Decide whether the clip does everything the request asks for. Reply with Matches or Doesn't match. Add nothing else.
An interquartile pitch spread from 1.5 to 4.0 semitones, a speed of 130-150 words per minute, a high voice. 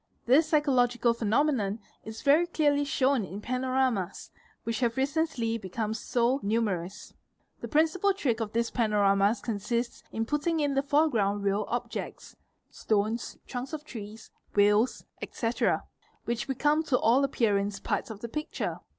Doesn't match